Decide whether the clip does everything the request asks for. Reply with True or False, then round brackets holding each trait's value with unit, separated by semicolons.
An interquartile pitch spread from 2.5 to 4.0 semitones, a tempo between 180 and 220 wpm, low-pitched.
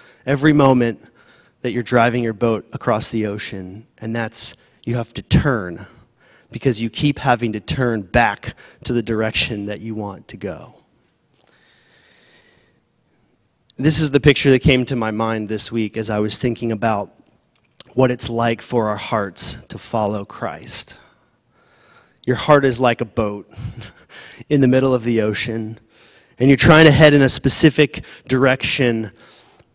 False (3.1 semitones; 155 wpm; 120 Hz)